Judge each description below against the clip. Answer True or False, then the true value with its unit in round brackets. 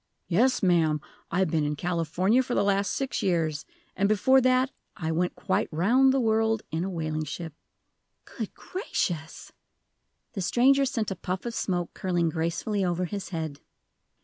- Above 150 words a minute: True (160 wpm)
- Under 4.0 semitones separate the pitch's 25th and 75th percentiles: False (5.2 semitones)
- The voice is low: False (185 Hz)